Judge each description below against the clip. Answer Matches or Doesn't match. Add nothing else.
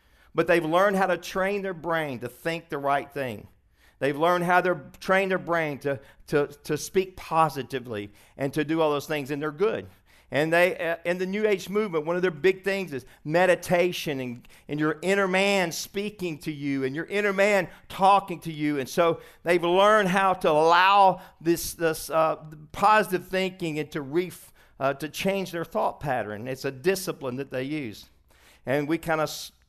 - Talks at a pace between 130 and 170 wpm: Doesn't match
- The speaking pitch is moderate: Matches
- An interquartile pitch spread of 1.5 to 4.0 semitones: Doesn't match